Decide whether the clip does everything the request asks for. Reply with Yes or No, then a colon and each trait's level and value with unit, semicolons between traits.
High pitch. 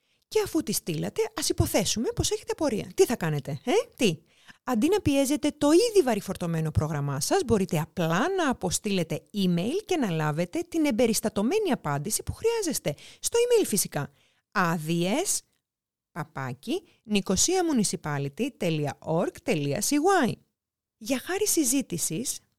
Yes: high, 220 Hz